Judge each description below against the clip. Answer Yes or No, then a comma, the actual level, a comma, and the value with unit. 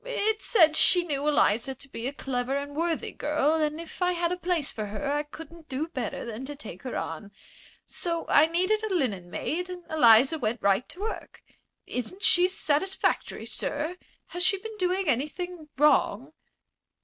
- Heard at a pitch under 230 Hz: No, very high, 305 Hz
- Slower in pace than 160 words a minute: No, average, 175 wpm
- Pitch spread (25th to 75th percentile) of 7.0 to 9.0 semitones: No, average, 5.2 semitones